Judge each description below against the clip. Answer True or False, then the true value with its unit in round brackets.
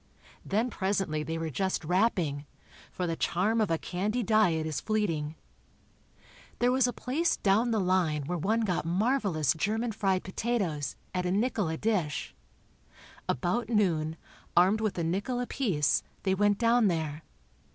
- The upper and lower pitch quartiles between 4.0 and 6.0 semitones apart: True (5.3 semitones)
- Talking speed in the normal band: True (150 wpm)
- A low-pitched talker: False (190 Hz)